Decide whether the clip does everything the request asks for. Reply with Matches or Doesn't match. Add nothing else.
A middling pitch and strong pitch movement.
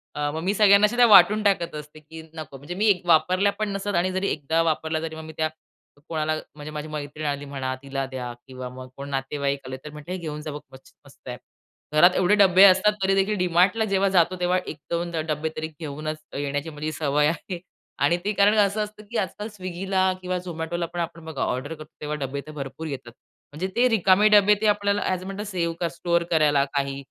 Doesn't match